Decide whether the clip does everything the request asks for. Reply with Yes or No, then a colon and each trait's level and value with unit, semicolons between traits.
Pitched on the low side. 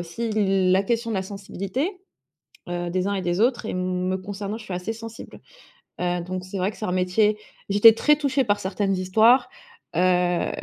No: high, 195 Hz